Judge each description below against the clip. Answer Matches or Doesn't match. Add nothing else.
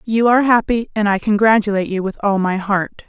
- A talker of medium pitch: Doesn't match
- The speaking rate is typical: Doesn't match